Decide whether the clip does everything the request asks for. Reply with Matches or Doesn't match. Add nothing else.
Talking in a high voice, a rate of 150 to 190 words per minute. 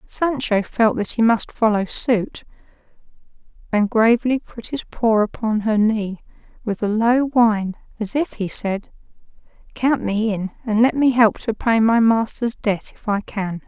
Matches